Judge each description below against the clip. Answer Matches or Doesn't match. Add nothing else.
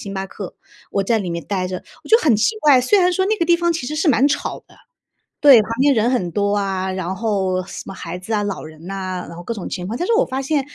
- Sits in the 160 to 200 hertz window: Doesn't match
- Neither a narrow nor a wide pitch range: Doesn't match